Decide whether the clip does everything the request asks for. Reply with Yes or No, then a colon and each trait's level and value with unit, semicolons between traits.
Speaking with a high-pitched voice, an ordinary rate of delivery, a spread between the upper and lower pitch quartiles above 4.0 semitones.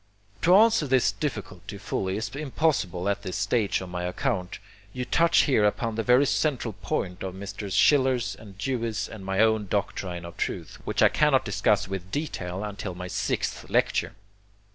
No: low, 105 Hz; average, 165 wpm; average, 5.2 semitones